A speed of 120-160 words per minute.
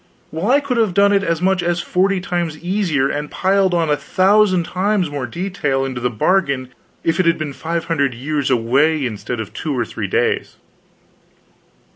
No: average, 185 wpm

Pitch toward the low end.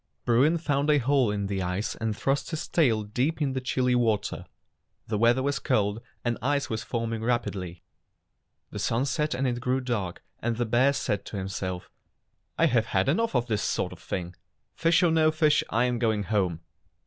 Yes: low, 120 Hz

